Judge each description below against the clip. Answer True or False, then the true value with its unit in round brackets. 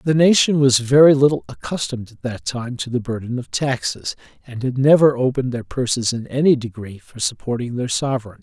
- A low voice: True (125 Hz)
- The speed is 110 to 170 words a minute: False (190 wpm)